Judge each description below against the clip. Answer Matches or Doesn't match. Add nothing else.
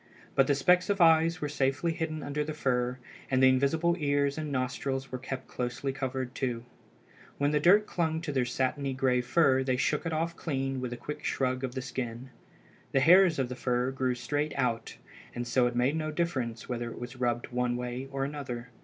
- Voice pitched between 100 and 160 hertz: Matches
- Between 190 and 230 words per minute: Matches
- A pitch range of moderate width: Matches